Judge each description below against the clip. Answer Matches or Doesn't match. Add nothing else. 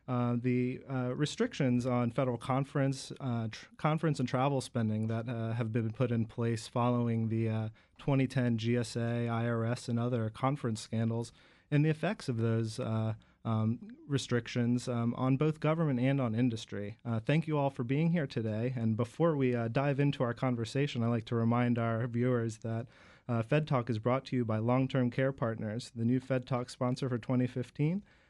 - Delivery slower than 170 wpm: Doesn't match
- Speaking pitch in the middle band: Doesn't match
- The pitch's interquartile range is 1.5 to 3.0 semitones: Matches